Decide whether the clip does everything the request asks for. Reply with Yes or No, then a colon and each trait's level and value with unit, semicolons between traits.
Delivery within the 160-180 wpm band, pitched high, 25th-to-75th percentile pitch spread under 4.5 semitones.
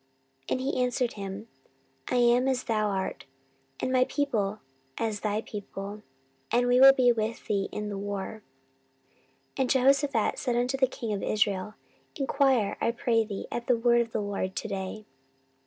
Yes: average, 170 wpm; high, 230 Hz; average, 3.5 semitones